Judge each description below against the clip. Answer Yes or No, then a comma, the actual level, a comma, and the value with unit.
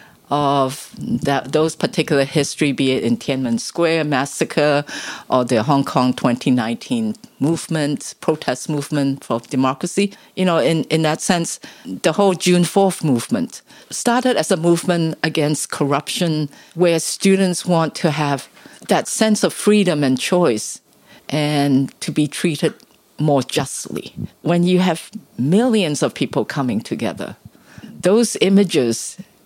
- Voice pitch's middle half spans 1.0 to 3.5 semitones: No, average, 4.4 semitones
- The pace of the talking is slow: Yes, slow, 130 wpm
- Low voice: No, medium, 160 Hz